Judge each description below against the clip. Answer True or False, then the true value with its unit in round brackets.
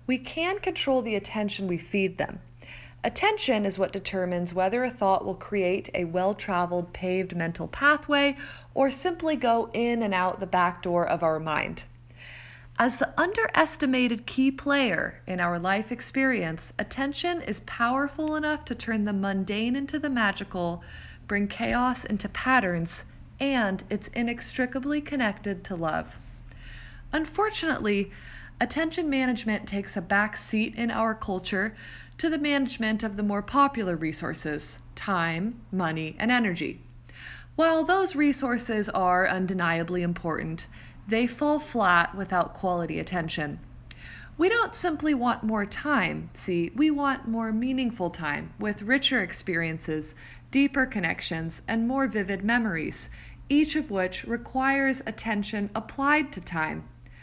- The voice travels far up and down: True (6.7 semitones)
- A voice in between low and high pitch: False (215 Hz)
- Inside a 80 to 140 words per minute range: True (135 wpm)